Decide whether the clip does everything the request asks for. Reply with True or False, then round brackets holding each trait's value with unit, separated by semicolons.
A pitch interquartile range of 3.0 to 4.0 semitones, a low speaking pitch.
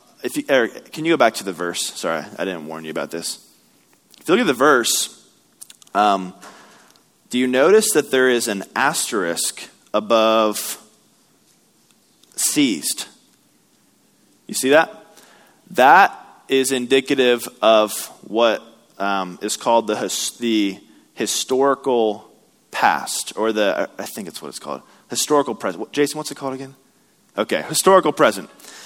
False (5.0 semitones; 120 Hz)